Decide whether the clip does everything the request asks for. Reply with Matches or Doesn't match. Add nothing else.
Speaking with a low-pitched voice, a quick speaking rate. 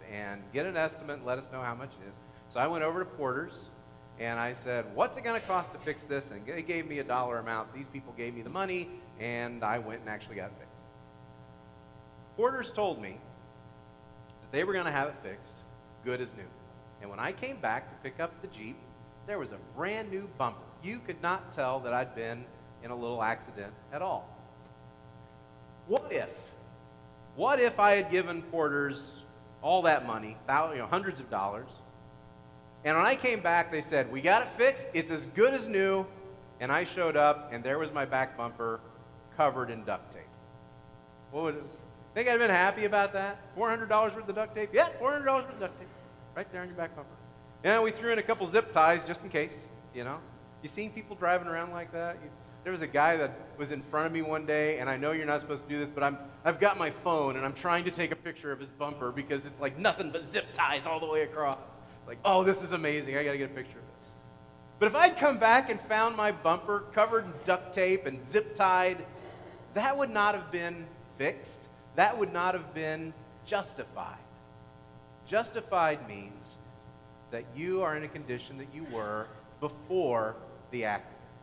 Doesn't match